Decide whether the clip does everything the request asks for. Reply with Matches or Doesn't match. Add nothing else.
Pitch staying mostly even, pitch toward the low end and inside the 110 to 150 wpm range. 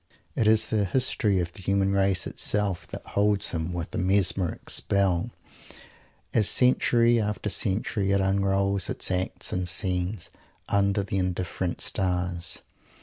Matches